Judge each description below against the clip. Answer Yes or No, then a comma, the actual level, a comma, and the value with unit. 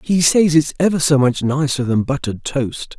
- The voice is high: No, medium, 145 Hz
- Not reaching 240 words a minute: Yes, average, 200 wpm